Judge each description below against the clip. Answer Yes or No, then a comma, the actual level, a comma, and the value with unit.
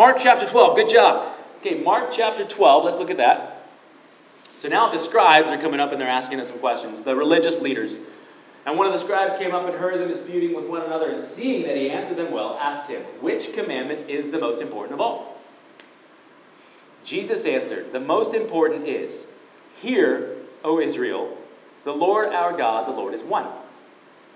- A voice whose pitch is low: No, high, 195 Hz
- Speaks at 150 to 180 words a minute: No, average, 190 wpm